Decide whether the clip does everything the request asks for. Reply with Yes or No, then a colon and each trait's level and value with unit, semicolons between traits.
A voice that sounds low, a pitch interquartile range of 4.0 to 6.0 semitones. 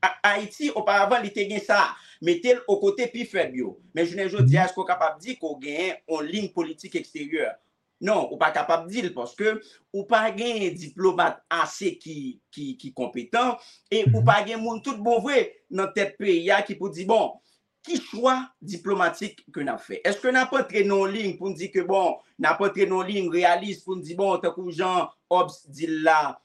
No: high, 195 Hz; average, 4.4 semitones